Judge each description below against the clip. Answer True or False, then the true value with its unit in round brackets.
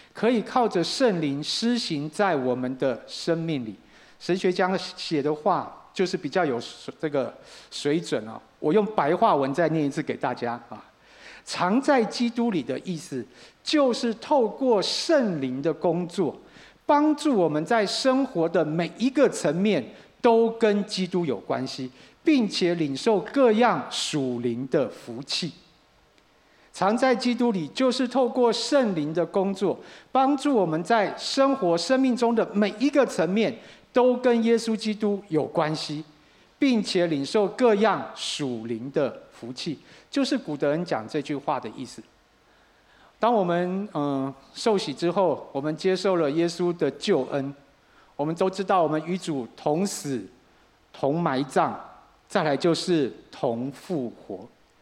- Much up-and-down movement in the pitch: True (7.4 semitones)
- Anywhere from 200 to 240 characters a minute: True (210 characters per minute)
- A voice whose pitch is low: False (185 Hz)